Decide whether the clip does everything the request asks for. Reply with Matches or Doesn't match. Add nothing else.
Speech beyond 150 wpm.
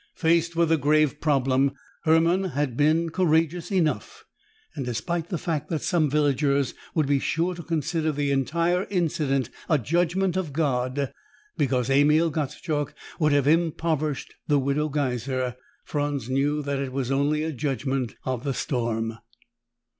Doesn't match